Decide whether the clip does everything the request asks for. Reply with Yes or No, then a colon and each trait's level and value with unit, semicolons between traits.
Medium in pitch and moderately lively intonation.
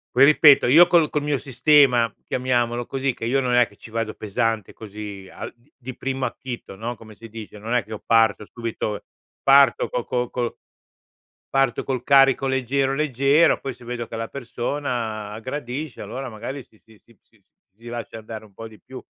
No: low, 120 Hz; average, 3.2 semitones